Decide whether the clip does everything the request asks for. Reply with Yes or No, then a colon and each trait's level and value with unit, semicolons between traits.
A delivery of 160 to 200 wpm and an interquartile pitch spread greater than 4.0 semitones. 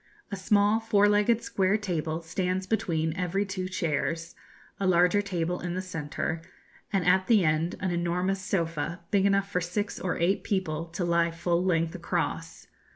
No: average, 165 wpm; average, 2.8 semitones